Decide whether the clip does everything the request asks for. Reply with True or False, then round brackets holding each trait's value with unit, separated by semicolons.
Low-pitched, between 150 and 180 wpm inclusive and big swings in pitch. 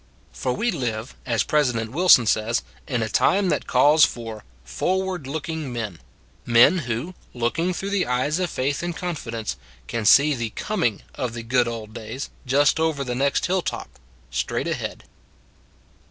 True (130 Hz; 170 wpm; 5.8 semitones)